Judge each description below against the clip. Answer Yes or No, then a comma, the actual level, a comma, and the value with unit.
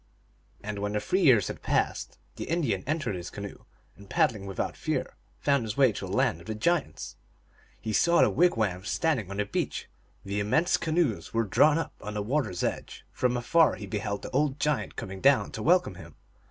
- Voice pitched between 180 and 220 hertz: No, low, 110 Hz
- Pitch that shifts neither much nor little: No, wide, 6.9 semitones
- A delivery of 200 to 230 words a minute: Yes, fast, 205 wpm